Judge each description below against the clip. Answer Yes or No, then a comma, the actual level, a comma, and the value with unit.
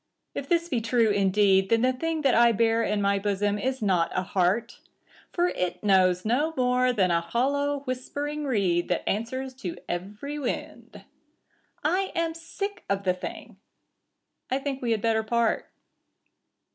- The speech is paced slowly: No, average, 160 wpm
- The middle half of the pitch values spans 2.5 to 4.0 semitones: No, wide, 5.5 semitones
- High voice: Yes, high, 230 Hz